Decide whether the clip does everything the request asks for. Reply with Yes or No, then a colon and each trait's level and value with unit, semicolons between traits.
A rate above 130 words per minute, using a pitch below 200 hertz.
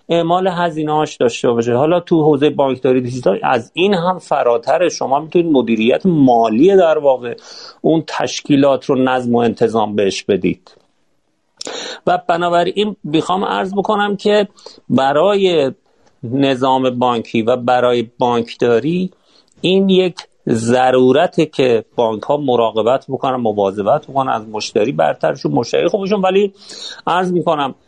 No: average, 125 wpm; medium, 140 Hz